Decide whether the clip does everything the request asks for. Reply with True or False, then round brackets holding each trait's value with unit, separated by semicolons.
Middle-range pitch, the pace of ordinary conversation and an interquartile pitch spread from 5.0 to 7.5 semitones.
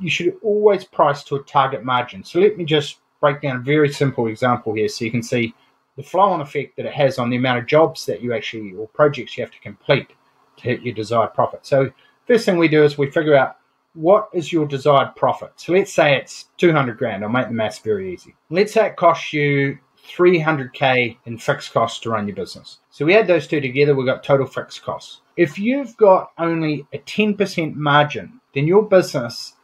False (145 Hz; 220 wpm; 5.5 semitones)